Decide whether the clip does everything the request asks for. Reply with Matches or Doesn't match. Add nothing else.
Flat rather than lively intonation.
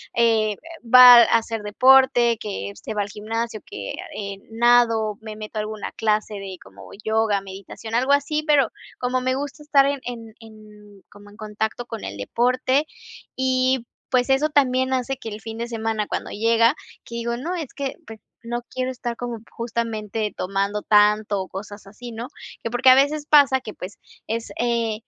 Doesn't match